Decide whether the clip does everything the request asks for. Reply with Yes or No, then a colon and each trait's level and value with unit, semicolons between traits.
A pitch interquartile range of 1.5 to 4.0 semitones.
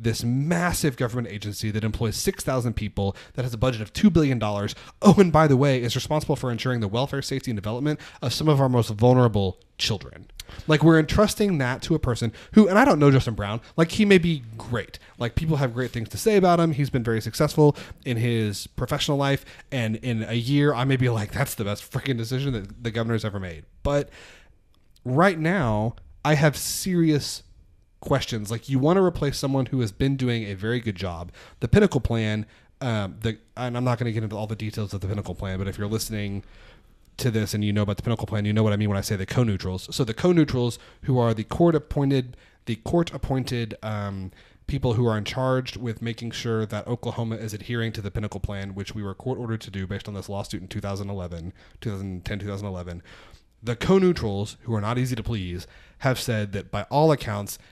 No: average, 4.5 semitones